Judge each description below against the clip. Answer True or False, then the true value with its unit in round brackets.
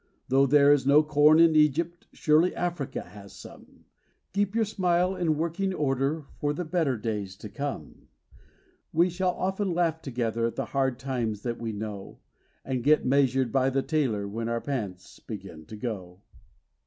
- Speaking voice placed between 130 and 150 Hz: True (135 Hz)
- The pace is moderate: True (165 wpm)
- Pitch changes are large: True (6.0 semitones)